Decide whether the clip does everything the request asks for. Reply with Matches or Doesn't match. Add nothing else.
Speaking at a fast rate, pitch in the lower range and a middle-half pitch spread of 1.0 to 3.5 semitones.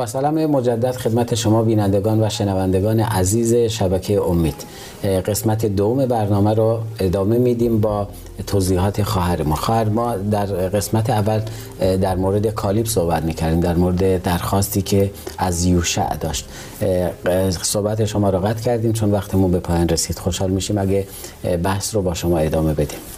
Doesn't match